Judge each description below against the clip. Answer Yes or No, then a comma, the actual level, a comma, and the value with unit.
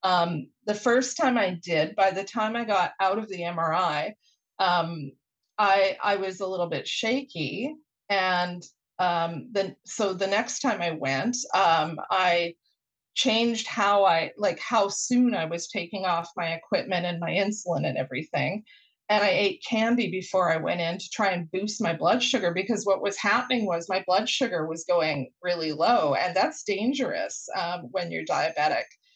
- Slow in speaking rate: No, average, 175 wpm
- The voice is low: No, high, 195 Hz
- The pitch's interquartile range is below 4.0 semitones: No, average, 4.4 semitones